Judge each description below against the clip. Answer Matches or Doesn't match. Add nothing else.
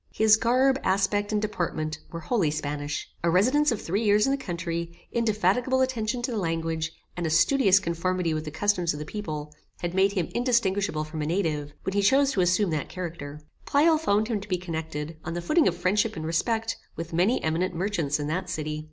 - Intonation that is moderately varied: Matches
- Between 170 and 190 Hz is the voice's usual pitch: Matches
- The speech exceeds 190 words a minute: Matches